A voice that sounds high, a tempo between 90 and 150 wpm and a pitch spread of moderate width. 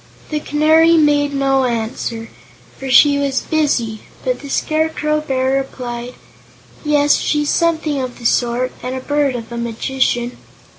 Yes: very high, 270 Hz; average, 145 wpm; average, 3.5 semitones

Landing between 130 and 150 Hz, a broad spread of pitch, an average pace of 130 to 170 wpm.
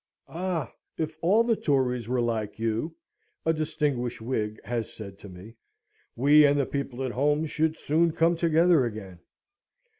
Yes: medium, 140 Hz; wide, 5.7 semitones; average, 155 wpm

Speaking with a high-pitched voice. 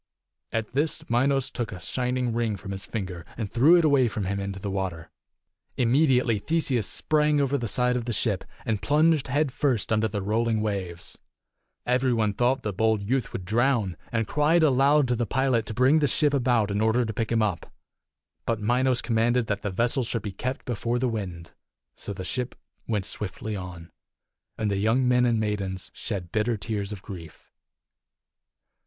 No: low, 115 Hz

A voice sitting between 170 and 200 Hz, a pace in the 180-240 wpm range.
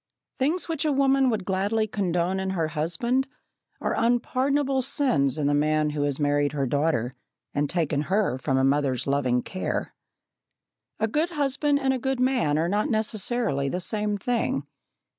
No: high, 190 Hz; average, 165 wpm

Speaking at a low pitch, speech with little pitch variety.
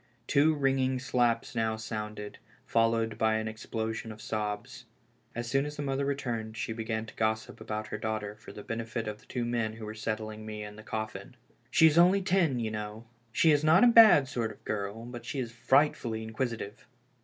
No: low, 115 Hz; average, 3.3 semitones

